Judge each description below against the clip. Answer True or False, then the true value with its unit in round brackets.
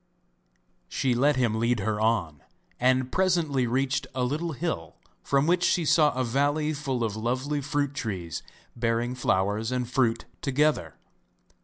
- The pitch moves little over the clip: False (4.2 semitones)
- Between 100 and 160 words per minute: True (145 wpm)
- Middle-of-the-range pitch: False (130 Hz)